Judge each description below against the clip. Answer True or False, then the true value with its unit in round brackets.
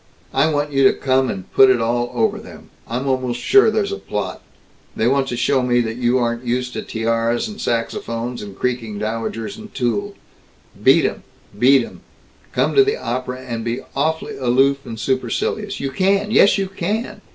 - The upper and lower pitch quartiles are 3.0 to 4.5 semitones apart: False (5.1 semitones)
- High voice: False (130 Hz)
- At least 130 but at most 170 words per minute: False (185 wpm)